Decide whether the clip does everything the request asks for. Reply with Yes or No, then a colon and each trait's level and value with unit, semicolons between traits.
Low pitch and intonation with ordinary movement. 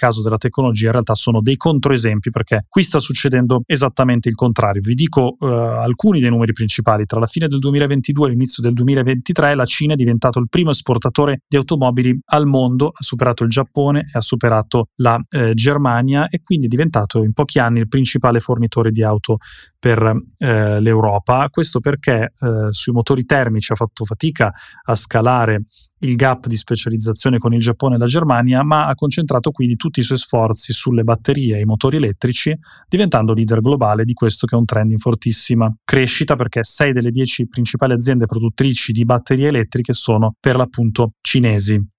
Yes: low, 125 Hz; average, 3.1 semitones